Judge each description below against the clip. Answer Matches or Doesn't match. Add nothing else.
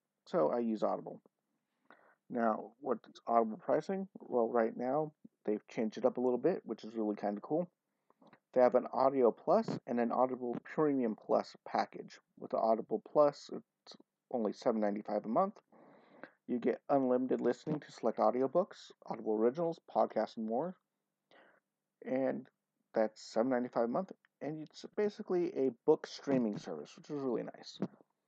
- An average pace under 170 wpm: Matches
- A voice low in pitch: Matches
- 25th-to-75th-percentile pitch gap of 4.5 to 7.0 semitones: Matches